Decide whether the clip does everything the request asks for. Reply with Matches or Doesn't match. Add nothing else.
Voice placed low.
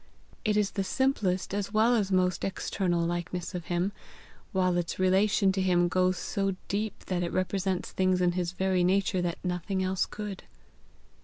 Doesn't match